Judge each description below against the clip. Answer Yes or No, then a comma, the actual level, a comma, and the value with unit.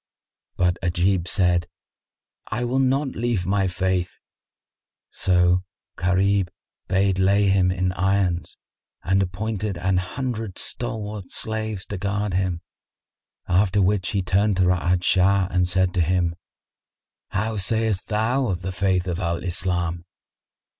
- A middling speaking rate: No, slow, 130 wpm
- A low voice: Yes, very low, 95 Hz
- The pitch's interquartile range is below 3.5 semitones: Yes, narrow, 2.4 semitones